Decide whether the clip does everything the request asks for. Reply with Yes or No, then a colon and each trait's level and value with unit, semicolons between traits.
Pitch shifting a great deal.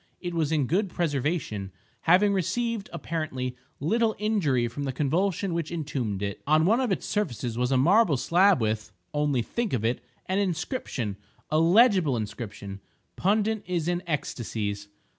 Yes: wide, 7.8 semitones